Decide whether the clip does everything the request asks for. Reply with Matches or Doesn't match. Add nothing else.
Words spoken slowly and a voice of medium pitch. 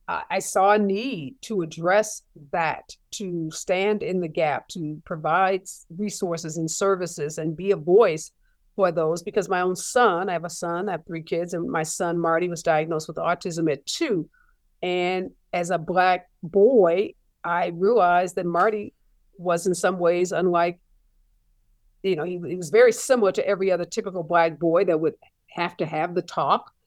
Doesn't match